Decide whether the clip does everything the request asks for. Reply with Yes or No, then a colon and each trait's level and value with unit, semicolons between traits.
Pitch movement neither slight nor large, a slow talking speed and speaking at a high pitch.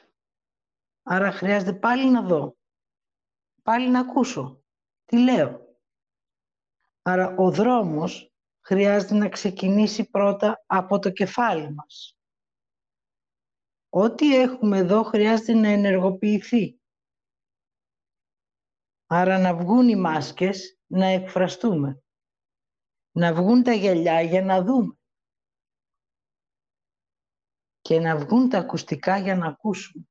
Yes: average, 3.6 semitones; slow, 100 wpm; high, 195 Hz